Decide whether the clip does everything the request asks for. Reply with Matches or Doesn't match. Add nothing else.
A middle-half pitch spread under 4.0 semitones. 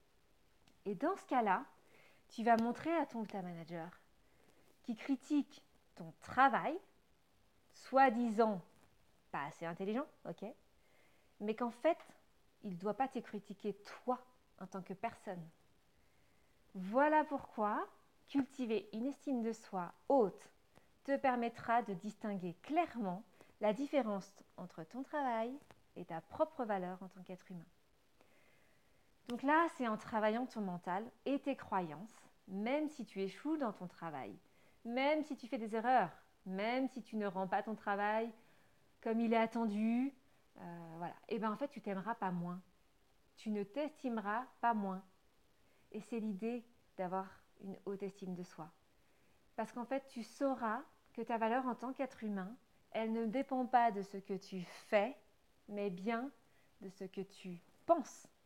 Doesn't match